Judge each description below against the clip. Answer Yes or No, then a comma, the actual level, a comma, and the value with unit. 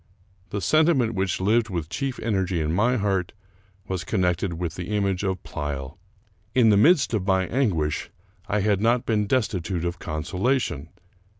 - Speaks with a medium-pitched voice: No, very low, 95 Hz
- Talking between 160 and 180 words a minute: Yes, average, 165 wpm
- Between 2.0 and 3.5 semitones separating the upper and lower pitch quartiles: No, average, 4.3 semitones